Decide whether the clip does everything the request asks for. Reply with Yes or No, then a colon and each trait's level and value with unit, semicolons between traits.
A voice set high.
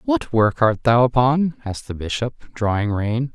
No: low, 115 Hz